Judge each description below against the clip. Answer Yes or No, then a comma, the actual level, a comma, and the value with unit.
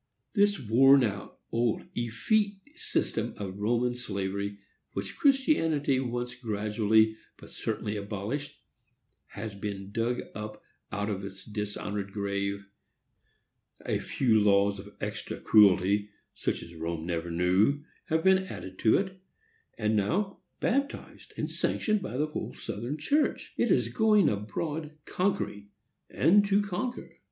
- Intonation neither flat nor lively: No, wide, 7.4 semitones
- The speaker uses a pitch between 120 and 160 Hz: No, low, 110 Hz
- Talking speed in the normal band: No, slow, 130 wpm